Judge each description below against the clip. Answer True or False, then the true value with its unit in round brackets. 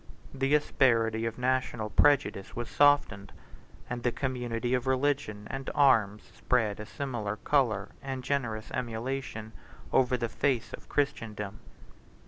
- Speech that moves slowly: True (125 wpm)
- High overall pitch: False (120 Hz)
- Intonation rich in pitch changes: False (3.5 semitones)